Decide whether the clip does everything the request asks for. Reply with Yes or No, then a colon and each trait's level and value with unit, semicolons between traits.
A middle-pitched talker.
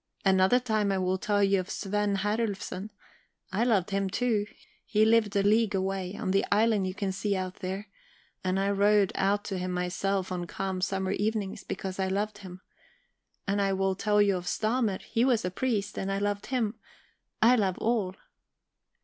No: high, 200 Hz